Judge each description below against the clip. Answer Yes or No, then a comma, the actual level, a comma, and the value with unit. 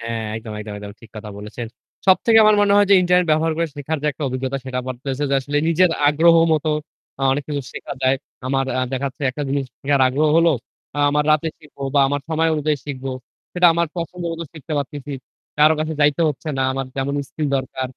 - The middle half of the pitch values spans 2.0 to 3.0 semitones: No, average, 3.4 semitones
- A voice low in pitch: No, medium, 145 Hz